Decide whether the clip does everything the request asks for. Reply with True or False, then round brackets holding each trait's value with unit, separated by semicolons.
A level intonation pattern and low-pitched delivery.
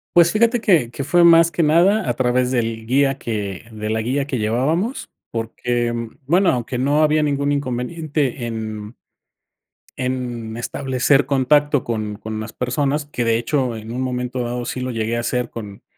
False (4.0 semitones; 125 Hz)